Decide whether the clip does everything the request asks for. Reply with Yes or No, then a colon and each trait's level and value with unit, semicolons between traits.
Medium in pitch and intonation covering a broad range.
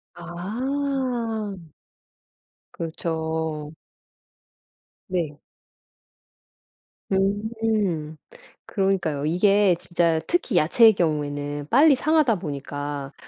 Yes: medium, 175 Hz; wide, 6.2 semitones